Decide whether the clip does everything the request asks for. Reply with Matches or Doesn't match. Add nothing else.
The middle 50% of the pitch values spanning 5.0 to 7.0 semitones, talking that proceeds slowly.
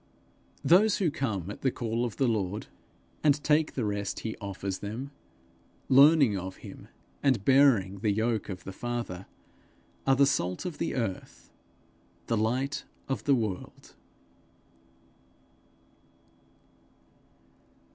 Matches